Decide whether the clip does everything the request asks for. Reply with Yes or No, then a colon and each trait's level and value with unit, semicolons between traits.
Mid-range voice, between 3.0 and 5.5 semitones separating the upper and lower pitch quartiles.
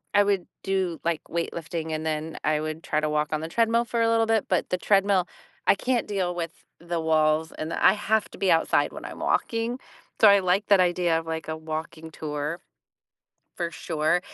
Yes: medium, 170 Hz; average, 4.0 semitones